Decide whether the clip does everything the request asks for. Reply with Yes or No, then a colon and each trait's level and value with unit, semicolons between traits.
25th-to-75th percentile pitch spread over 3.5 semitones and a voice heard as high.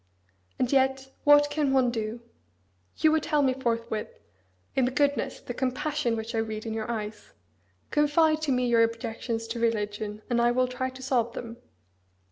No: average, 2.9 semitones; high, 245 Hz